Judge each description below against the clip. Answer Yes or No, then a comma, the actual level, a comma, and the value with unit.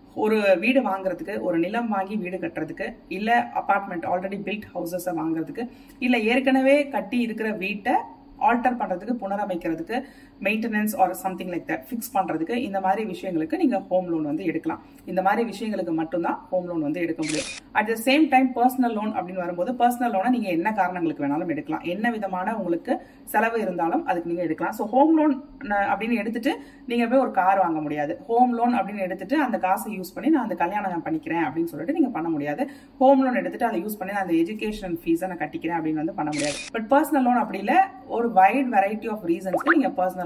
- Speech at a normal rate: No, fast, 160 wpm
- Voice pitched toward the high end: Yes, high, 205 Hz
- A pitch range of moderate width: No, wide, 6.1 semitones